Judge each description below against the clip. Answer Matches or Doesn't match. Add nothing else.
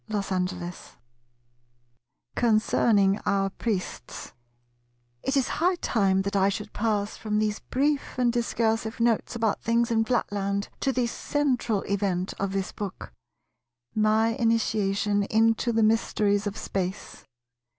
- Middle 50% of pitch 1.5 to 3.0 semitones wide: Matches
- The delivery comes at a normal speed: Doesn't match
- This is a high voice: Matches